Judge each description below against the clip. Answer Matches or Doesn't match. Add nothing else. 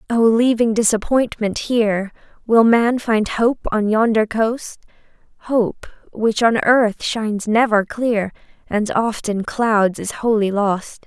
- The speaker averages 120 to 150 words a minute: Matches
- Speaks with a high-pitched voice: Matches